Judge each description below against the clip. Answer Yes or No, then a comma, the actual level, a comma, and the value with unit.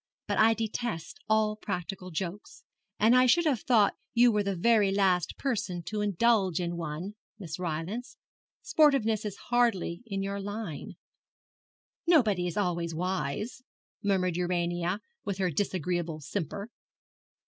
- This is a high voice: Yes, high, 195 Hz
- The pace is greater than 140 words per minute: No, slow, 135 wpm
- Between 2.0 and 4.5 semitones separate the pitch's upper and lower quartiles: Yes, average, 3.9 semitones